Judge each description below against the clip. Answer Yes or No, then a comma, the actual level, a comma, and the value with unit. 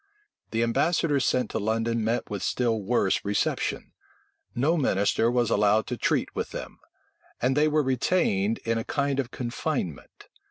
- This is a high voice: No, low, 120 Hz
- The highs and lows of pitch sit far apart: No, average, 3.9 semitones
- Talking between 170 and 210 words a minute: No, average, 155 wpm